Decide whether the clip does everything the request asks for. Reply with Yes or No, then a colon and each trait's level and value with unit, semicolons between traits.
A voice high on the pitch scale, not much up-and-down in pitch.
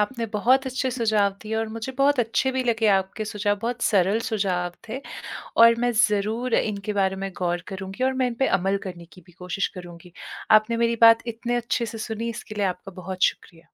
No: high, 215 Hz; average, 3.4 semitones